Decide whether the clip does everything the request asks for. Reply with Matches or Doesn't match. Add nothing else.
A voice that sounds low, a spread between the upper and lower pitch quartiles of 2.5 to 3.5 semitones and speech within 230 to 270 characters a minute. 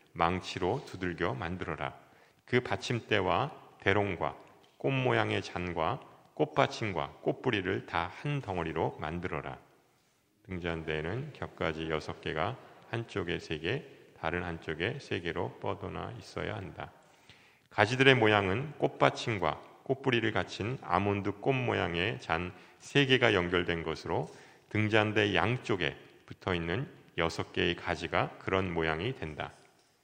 Doesn't match